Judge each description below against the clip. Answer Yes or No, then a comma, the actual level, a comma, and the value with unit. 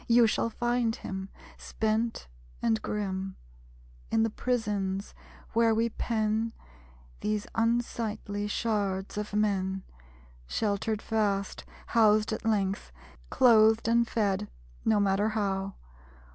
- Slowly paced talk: Yes, slow, 105 wpm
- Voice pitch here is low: No, high, 215 Hz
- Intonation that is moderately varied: No, narrow, 2.2 semitones